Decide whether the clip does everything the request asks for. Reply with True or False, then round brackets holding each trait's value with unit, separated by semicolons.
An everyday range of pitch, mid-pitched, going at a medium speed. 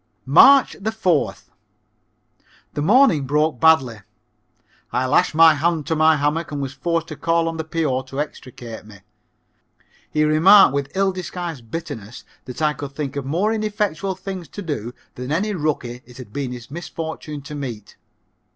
True (4.1 semitones; 155 Hz; 160 wpm)